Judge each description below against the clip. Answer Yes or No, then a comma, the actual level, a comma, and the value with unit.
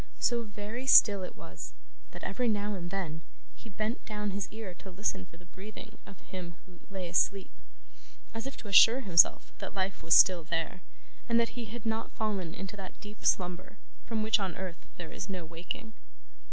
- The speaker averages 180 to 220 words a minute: Yes, average, 190 wpm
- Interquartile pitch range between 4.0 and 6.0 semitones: No, average, 3.3 semitones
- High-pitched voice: Yes, high, 195 Hz